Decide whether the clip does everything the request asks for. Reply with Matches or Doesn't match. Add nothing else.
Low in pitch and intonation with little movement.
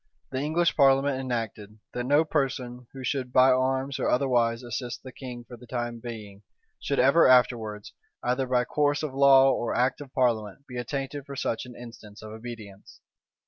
Matches